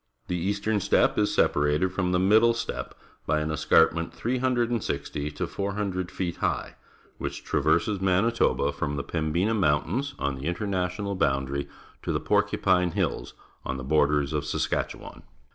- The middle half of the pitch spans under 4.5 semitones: No, wide, 5.4 semitones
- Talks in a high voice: No, very low, 90 Hz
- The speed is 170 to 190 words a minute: No, average, 160 wpm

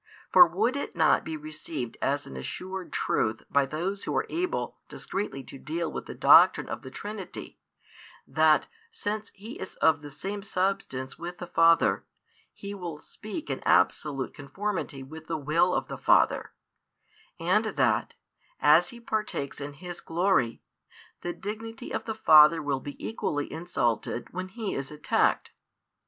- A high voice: No, medium, 165 Hz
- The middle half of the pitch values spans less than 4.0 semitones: No, wide, 5.5 semitones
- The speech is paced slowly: No, average, 155 wpm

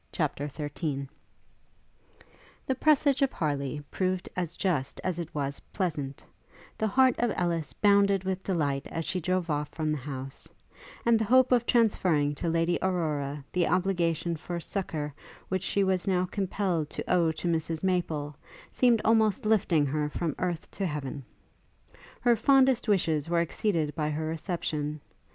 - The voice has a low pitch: No, medium, 170 Hz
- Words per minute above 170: No, average, 155 wpm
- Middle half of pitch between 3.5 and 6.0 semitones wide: Yes, average, 4.6 semitones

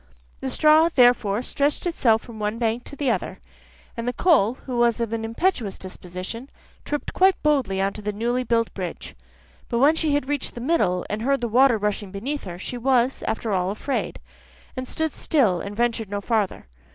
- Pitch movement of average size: Yes, average, 4.9 semitones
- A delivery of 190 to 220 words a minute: Yes, average, 195 wpm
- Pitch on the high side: Yes, high, 235 Hz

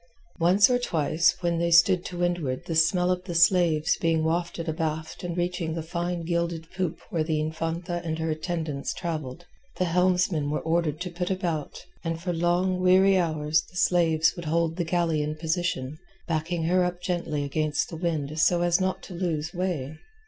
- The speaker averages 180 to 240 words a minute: Yes, average, 185 wpm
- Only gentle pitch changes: Yes, narrow, 2.0 semitones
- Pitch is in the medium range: Yes, medium, 170 Hz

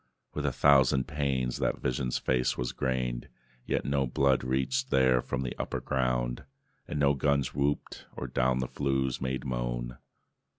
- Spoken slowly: No, average, 160 wpm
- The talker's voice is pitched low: Yes, very low, 65 Hz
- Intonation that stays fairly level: Yes, narrow, 1.6 semitones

